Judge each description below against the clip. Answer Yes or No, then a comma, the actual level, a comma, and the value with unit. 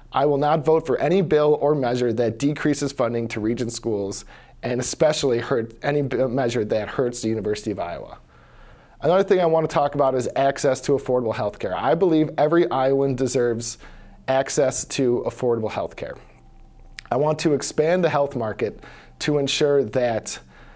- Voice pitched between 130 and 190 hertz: Yes, low, 135 Hz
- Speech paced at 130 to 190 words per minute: Yes, average, 170 wpm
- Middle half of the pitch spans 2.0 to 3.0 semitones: No, average, 4.0 semitones